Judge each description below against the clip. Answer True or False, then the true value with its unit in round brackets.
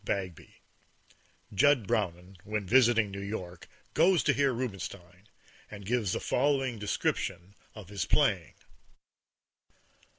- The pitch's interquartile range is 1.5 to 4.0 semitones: False (4.6 semitones)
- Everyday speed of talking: False (110 wpm)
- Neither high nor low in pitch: False (105 Hz)